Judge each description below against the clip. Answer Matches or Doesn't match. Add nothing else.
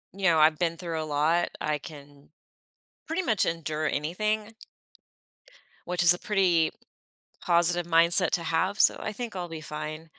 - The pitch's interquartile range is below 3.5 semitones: Matches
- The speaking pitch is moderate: Matches